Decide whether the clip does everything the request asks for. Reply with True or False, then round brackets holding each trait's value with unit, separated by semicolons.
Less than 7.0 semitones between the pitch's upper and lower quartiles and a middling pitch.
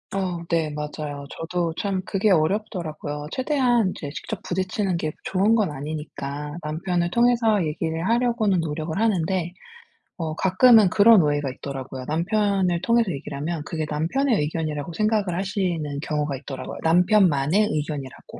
True (5.1 semitones; 170 Hz)